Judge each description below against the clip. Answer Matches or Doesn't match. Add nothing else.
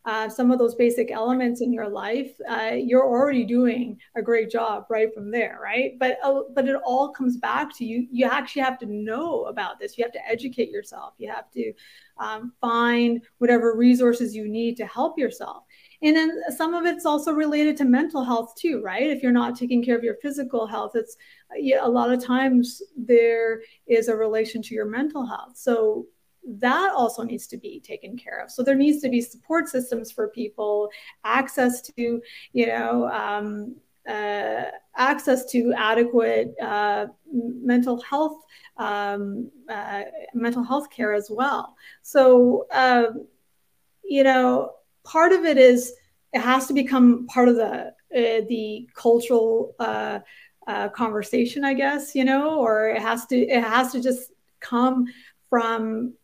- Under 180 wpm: Matches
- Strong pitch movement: Doesn't match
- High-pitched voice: Matches